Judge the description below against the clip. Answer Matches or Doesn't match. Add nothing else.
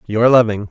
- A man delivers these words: Matches